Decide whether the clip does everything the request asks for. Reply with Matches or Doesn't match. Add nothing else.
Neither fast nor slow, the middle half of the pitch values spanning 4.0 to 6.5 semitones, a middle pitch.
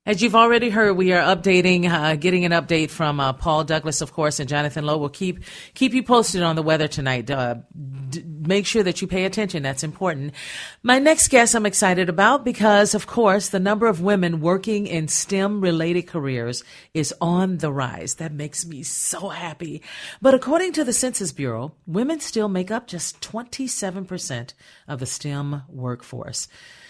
Matches